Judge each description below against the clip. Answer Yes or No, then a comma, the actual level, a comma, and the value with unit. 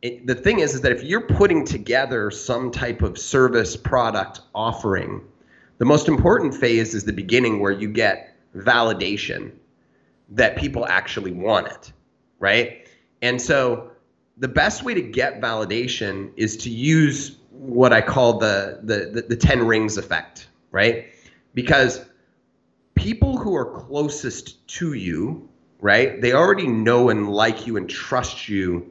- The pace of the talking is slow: No, average, 150 wpm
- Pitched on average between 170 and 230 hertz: No, low, 115 Hz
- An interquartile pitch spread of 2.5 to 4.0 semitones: Yes, average, 2.8 semitones